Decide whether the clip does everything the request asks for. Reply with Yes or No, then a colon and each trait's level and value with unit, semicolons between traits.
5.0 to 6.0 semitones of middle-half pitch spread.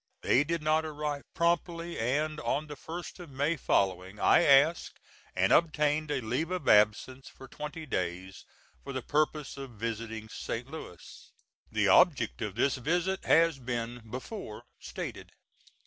Yes: wide, 5.4 semitones